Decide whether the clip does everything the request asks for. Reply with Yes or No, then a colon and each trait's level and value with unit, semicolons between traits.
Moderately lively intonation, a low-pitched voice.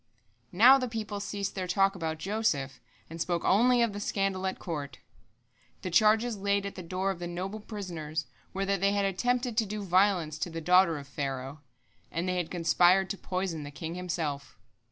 No: average, 3.5 semitones; medium, 185 Hz